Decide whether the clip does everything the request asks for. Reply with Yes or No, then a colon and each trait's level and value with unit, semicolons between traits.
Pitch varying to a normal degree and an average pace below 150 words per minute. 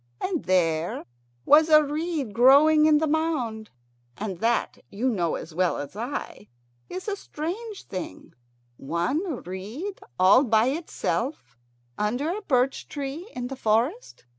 No: wide, 7.4 semitones; average, 140 wpm